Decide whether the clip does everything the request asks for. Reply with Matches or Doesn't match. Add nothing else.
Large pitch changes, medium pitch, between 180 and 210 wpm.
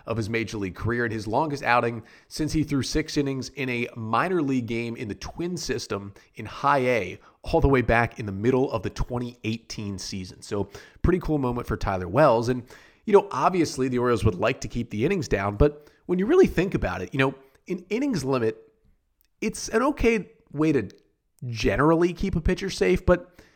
Doesn't match